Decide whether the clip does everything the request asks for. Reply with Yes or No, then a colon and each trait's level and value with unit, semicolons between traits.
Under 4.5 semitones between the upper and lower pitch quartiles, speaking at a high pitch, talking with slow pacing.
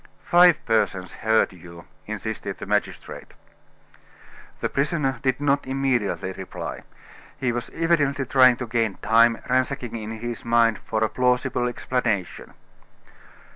No: average, 3.2 semitones; low, 120 Hz; slow, 125 wpm